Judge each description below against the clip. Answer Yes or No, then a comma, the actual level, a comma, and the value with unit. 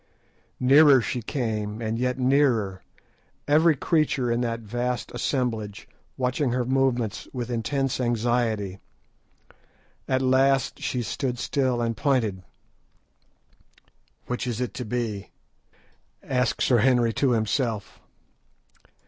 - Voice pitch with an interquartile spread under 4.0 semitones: Yes, narrow, 2.5 semitones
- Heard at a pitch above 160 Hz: No, low, 125 Hz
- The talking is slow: Yes, slow, 110 wpm